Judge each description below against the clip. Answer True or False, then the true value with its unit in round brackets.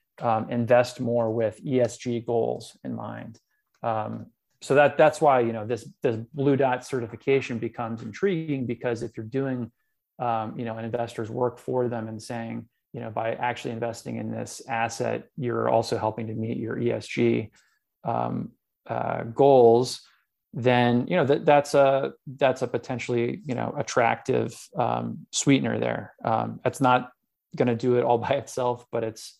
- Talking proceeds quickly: False (165 wpm)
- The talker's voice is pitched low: True (120 Hz)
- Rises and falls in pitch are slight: True (1.9 semitones)